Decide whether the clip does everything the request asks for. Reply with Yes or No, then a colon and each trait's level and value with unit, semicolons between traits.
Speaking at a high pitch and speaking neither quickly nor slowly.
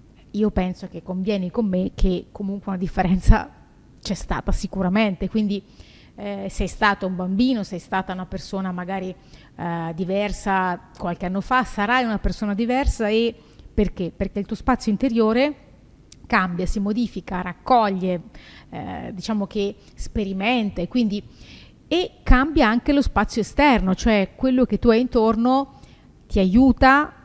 Yes: high, 205 Hz; average, 140 wpm